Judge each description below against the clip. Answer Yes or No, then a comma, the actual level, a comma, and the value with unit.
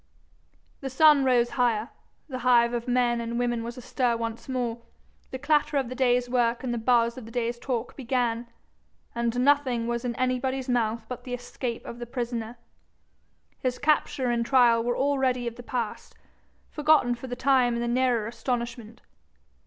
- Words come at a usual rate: Yes, average, 175 wpm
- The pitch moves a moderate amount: No, narrow, 1.4 semitones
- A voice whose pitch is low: No, high, 245 Hz